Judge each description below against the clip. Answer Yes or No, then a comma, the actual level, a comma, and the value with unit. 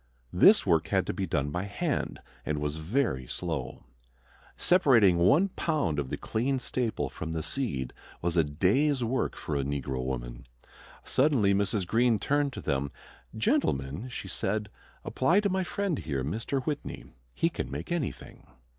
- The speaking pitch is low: Yes, low, 100 Hz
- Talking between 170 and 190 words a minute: No, average, 160 wpm